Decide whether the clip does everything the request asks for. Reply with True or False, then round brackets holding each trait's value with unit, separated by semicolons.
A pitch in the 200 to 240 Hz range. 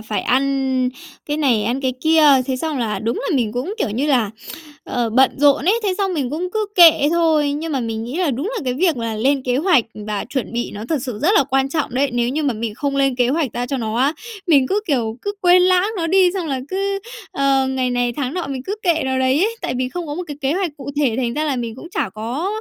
False (275 Hz)